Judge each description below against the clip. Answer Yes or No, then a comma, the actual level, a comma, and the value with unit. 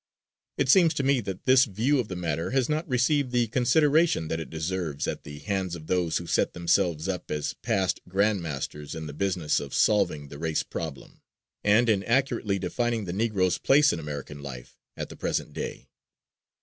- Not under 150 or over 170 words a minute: No, average, 190 wpm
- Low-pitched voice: Yes, very low, 95 Hz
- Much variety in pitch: Yes, wide, 7.1 semitones